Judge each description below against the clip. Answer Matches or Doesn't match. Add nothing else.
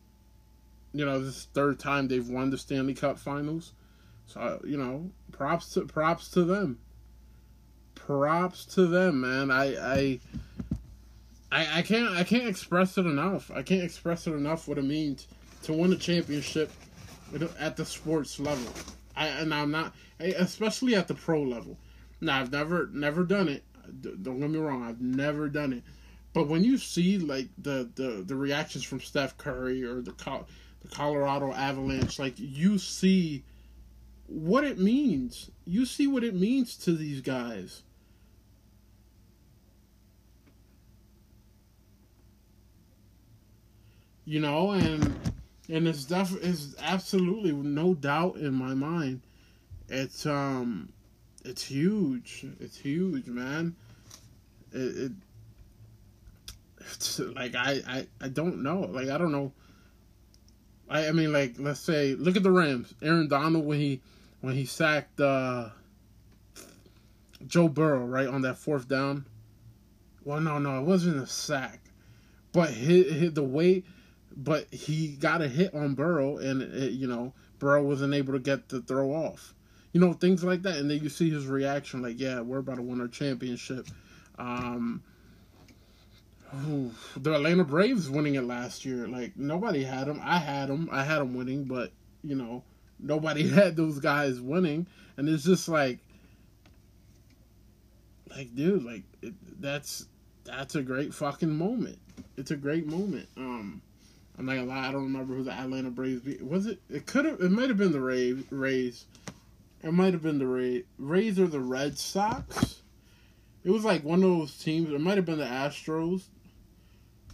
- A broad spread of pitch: Matches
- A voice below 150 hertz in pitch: Matches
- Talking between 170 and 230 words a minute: Doesn't match